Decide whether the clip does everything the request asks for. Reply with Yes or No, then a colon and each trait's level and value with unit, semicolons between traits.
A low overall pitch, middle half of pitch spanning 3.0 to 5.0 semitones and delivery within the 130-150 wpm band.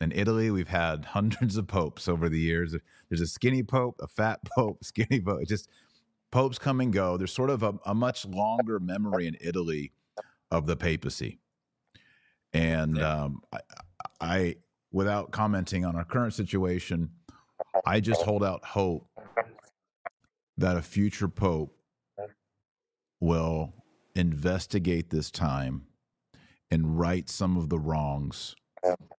Yes: very low, 90 Hz; average, 4.0 semitones; average, 140 wpm